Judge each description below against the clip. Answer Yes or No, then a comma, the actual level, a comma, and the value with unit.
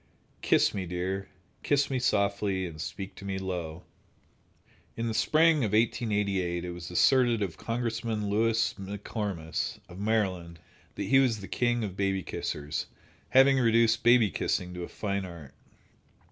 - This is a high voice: No, low, 100 Hz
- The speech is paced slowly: No, average, 155 wpm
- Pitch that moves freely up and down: No, average, 4.3 semitones